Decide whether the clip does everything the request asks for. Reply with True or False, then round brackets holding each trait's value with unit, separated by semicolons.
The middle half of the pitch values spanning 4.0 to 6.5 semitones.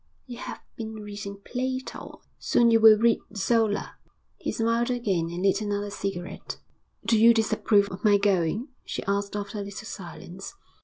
False (2.4 semitones)